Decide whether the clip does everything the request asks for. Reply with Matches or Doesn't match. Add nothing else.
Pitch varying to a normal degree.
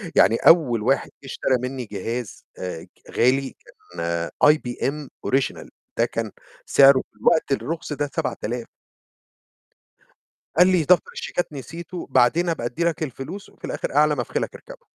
Matches